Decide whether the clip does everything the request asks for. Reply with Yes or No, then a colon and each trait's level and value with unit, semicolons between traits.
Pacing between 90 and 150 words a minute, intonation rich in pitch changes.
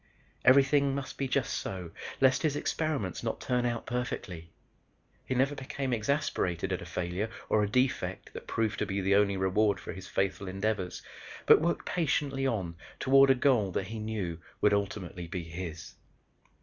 No: average, 170 wpm; wide, 6.1 semitones